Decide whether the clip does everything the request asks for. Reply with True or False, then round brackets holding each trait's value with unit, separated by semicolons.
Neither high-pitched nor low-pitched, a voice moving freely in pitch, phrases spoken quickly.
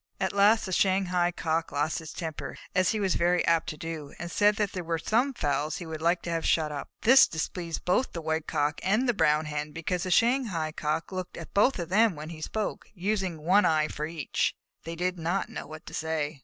False (170 Hz; 3.5 semitones; 235 wpm)